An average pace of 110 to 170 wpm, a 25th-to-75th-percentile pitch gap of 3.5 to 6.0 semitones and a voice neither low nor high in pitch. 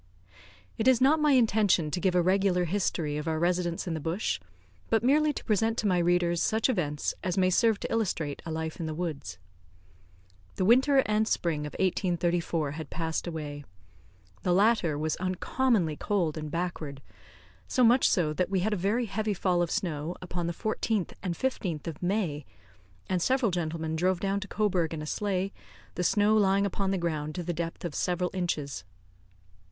No: average, 185 wpm; average, 4.1 semitones; medium, 180 Hz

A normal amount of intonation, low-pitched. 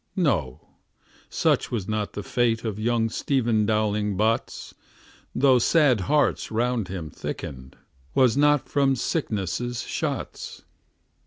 Yes: average, 3.7 semitones; low, 115 Hz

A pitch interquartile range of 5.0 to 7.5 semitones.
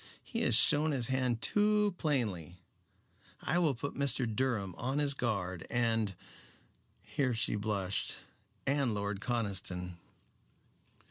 Yes: wide, 5.5 semitones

